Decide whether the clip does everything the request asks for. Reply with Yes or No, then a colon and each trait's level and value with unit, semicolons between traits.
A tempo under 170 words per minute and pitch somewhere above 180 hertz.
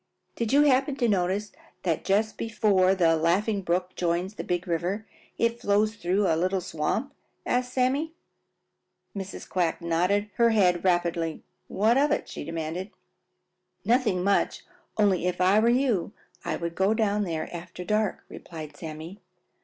Yes: average, 155 wpm; high, 190 Hz